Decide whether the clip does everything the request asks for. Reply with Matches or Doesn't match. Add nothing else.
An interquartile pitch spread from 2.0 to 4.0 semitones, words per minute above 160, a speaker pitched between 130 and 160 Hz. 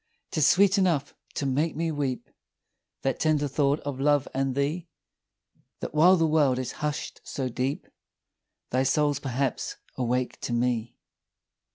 Doesn't match